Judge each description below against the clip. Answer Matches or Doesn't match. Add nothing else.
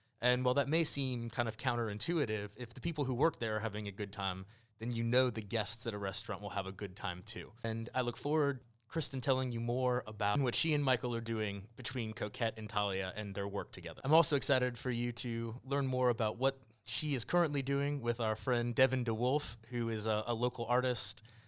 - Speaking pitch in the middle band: Doesn't match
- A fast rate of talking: Matches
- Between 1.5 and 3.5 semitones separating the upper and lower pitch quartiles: Matches